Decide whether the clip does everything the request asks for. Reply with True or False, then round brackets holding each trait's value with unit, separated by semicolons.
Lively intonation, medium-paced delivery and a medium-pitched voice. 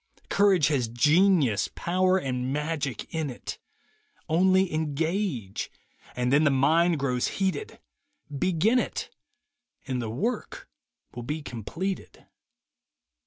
False (6.2 semitones; 115 wpm; 155 Hz)